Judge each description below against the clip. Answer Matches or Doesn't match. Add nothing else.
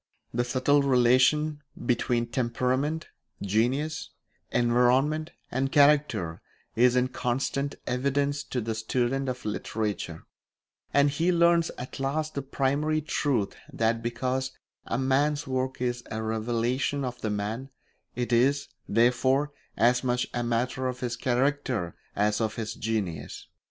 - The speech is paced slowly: Matches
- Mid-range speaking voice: Doesn't match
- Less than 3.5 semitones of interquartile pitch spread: Matches